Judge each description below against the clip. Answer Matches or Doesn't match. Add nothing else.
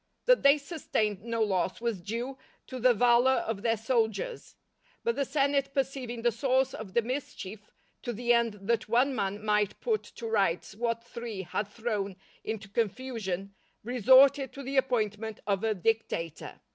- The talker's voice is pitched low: Doesn't match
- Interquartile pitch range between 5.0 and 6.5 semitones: Doesn't match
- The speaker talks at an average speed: Matches